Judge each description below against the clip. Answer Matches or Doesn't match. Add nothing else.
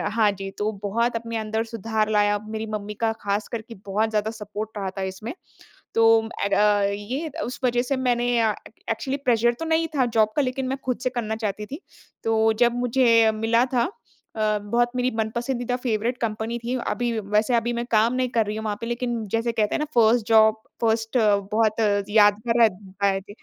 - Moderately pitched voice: Doesn't match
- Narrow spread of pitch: Matches